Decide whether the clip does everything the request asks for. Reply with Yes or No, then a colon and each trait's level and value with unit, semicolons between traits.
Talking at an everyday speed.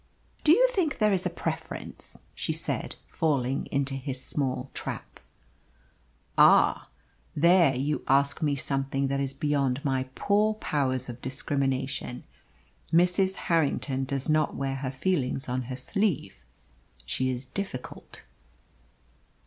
No: slow, 125 wpm